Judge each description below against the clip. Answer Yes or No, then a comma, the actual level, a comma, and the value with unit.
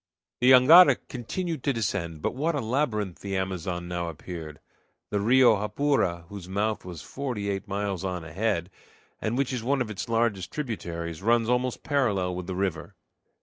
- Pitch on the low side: Yes, low, 105 Hz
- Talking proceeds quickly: No, average, 170 wpm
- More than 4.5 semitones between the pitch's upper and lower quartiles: Yes, wide, 5.6 semitones